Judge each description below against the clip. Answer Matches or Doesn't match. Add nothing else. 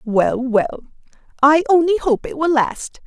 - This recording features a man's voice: Doesn't match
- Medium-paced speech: Matches